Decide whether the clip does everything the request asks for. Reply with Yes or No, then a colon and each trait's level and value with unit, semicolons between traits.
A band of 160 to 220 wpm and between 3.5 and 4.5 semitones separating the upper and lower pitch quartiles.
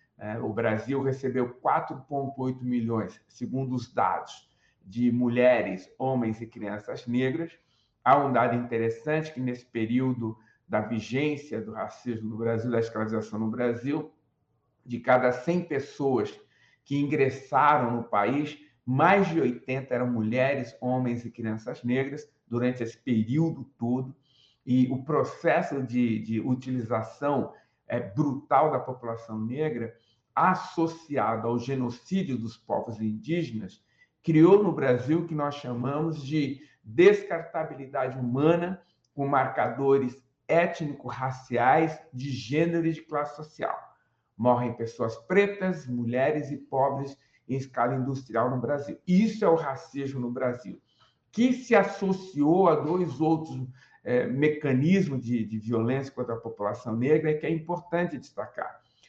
No: average, 125 wpm; average, 4.2 semitones